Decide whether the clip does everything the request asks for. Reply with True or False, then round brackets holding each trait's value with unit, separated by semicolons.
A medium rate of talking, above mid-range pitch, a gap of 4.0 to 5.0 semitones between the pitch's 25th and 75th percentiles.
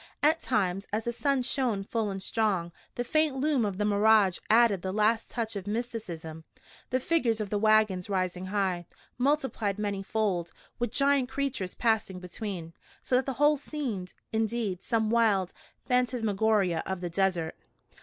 True (160 wpm; 215 Hz; 4.3 semitones)